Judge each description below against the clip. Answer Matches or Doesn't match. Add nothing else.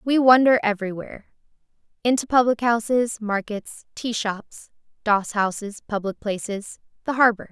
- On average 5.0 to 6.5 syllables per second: Doesn't match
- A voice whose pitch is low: Doesn't match